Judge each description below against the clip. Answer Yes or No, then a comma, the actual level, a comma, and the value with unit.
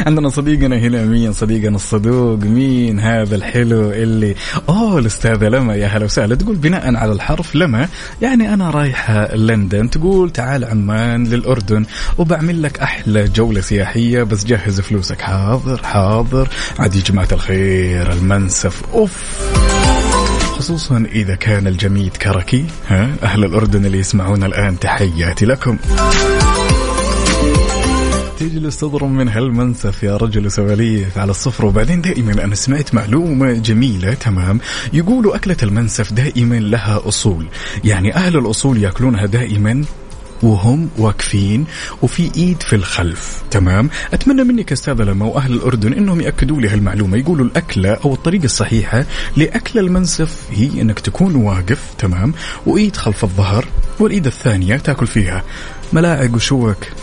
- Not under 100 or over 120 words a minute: No, average, 130 wpm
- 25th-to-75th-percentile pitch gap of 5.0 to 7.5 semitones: Yes, average, 5.3 semitones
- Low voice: Yes, low, 115 Hz